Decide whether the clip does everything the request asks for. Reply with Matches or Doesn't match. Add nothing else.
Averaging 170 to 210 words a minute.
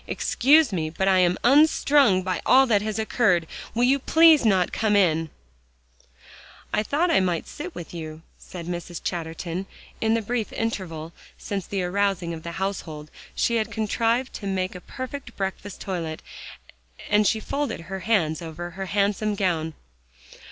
Doesn't match